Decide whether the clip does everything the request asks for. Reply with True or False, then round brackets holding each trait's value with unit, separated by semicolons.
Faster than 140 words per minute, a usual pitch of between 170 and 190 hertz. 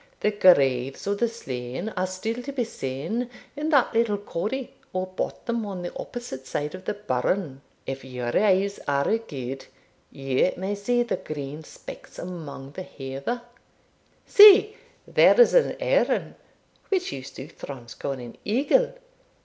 True (150 wpm; 185 Hz)